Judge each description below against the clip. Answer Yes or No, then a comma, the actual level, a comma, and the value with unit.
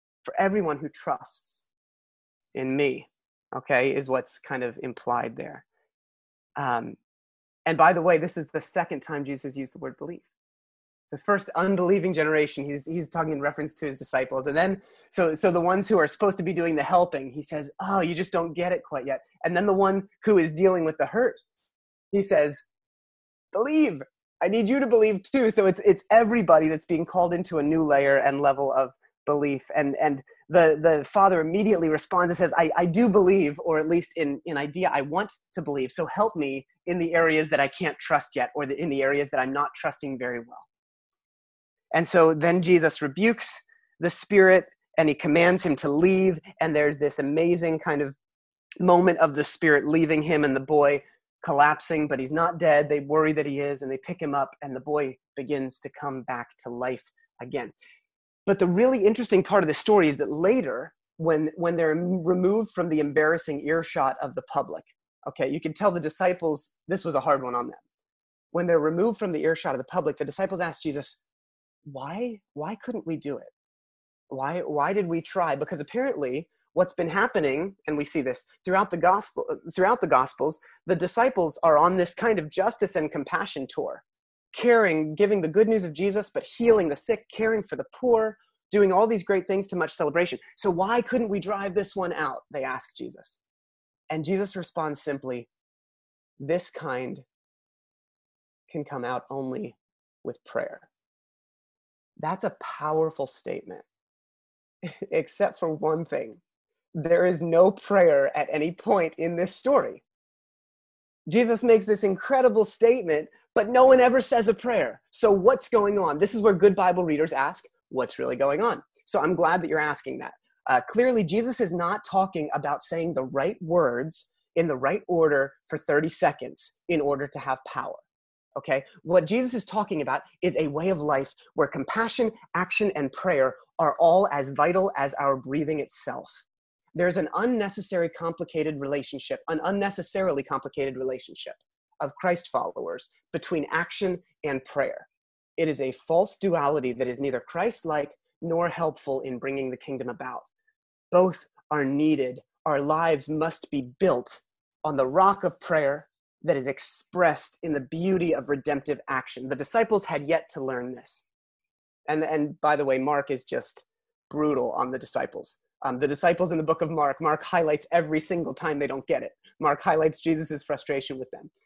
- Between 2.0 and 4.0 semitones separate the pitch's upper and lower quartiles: No, average, 5.0 semitones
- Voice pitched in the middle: Yes, medium, 165 Hz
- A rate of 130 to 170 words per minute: No, average, 185 wpm